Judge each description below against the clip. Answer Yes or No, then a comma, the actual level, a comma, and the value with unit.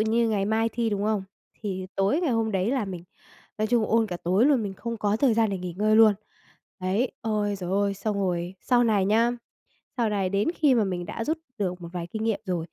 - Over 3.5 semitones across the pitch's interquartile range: No, average, 3.0 semitones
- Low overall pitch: No, high, 210 Hz